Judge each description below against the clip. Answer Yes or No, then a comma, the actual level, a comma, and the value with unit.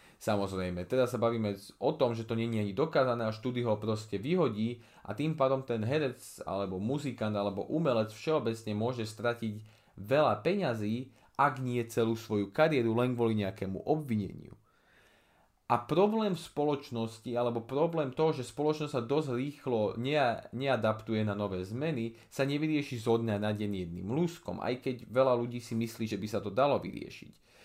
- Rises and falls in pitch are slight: No, average, 3.8 semitones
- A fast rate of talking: No, average, 165 wpm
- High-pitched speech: No, low, 115 Hz